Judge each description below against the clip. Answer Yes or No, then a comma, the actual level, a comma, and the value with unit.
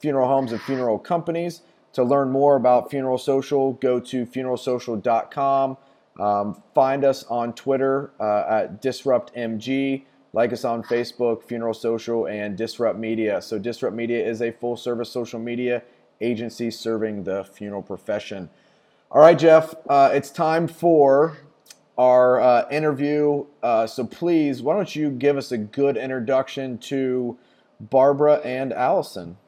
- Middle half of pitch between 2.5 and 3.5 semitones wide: Yes, average, 3.1 semitones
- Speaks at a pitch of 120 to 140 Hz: Yes, low, 125 Hz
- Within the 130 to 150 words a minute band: Yes, average, 140 wpm